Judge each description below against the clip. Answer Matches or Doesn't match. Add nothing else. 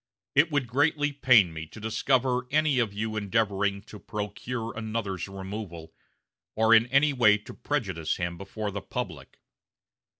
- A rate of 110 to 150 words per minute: Matches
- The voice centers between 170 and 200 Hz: Doesn't match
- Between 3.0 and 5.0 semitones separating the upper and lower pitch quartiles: Matches